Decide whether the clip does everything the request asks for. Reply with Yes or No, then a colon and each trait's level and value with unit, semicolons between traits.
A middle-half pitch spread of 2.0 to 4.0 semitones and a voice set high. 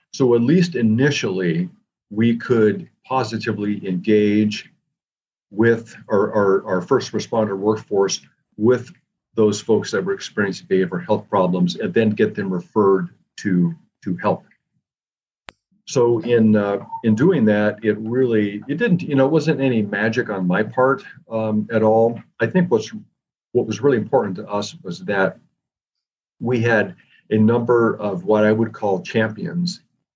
No: average, 3.2 semitones; low, 110 Hz